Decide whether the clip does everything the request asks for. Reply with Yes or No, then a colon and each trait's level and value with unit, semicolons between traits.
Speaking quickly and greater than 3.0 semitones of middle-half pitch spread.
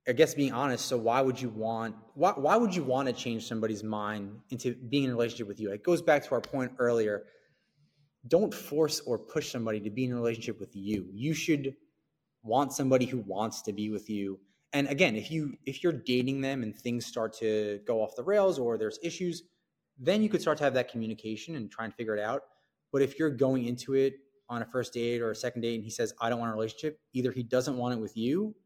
Yes: fast, 245 wpm; average, 4.2 semitones